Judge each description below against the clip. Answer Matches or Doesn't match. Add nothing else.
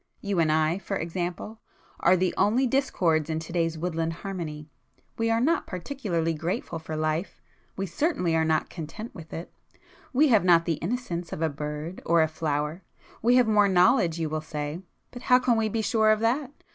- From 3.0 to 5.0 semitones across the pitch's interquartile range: Doesn't match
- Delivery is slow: Doesn't match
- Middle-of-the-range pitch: Matches